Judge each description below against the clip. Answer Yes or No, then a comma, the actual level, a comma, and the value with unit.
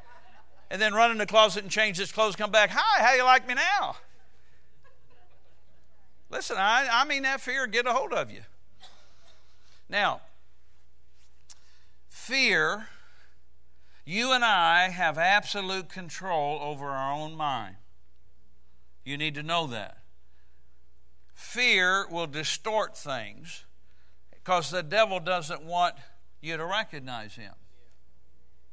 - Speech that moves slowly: Yes, slow, 125 wpm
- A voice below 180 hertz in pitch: Yes, low, 135 Hz